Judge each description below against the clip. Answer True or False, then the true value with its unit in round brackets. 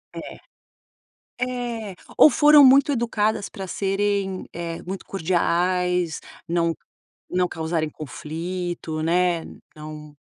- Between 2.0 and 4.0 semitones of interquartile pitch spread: True (3.6 semitones)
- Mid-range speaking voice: True (180 Hz)